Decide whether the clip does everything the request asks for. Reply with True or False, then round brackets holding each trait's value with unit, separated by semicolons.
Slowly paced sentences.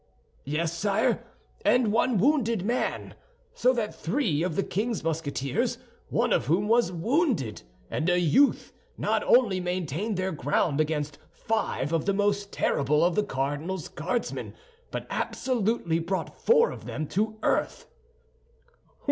True (130 wpm)